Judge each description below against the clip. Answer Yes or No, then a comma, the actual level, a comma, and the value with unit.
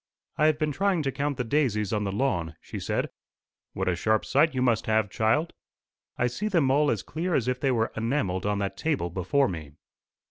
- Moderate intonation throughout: No, wide, 6.4 semitones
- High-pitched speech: No, low, 125 Hz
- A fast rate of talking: Yes, fast, 215 wpm